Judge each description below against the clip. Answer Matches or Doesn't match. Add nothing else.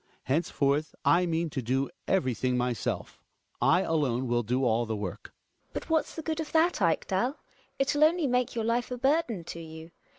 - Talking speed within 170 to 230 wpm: Matches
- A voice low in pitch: Doesn't match